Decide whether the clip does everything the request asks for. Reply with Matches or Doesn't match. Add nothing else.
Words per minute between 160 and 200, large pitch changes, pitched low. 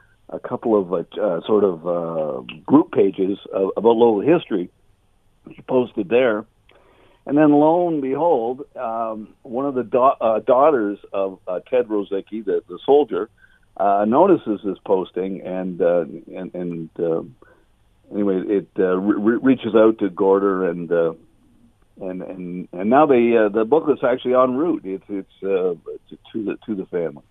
Matches